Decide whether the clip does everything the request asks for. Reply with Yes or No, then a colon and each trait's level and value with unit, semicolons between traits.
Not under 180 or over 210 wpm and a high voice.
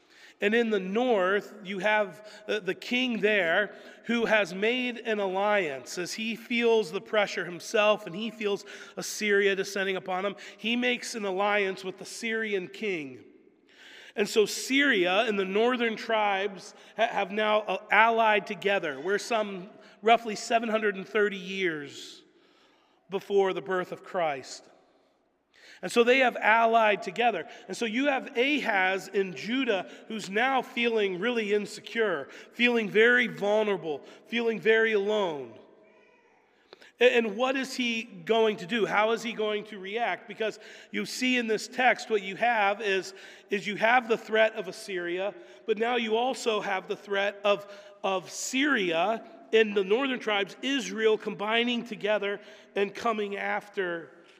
No: average, 145 wpm; high, 215 Hz